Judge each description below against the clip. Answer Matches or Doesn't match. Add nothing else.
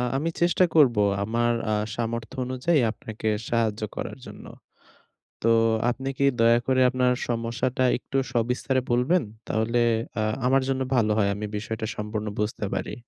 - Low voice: Matches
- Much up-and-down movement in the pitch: Doesn't match